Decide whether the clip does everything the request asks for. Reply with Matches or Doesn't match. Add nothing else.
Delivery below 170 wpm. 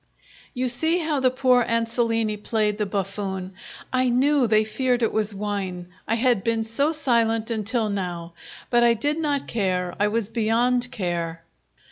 Matches